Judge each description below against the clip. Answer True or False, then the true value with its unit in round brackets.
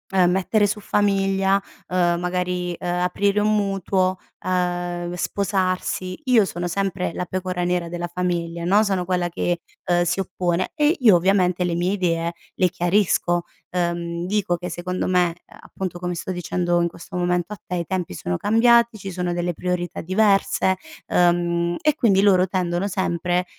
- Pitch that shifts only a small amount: True (1.8 semitones)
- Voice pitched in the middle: True (180 Hz)